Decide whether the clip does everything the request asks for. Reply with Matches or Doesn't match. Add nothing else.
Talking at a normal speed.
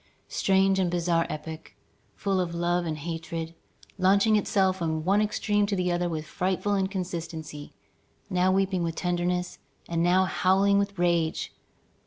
Matches